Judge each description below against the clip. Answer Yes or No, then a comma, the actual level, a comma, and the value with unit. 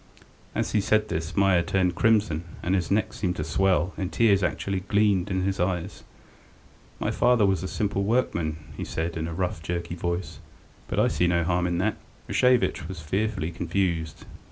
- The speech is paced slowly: No, average, 180 wpm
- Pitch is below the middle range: Yes, very low, 90 Hz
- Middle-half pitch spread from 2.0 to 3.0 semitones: Yes, narrow, 2.5 semitones